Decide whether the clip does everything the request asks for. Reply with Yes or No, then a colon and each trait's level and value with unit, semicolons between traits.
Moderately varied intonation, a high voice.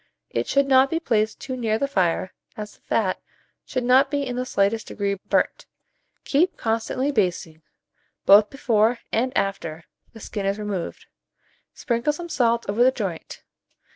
Yes: average, 4.6 semitones; high, 225 Hz